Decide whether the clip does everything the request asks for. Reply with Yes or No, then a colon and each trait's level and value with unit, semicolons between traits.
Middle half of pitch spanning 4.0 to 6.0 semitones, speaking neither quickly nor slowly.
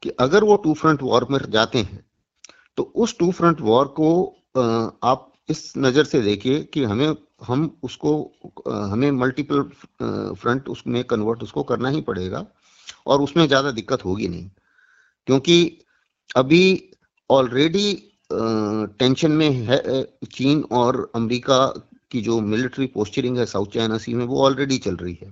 Yes: average, 4.9 semitones; average, 150 wpm